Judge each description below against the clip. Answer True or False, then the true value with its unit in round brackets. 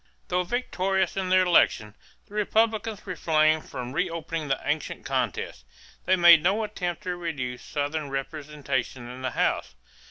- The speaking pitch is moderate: True (160 Hz)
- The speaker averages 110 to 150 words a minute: True (140 wpm)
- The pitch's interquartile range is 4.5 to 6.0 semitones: True (5.2 semitones)